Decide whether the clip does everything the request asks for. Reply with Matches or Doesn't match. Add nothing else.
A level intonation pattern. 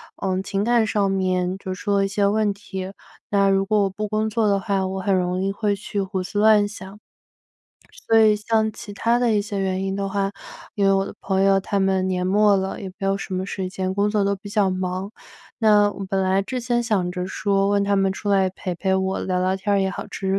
Matches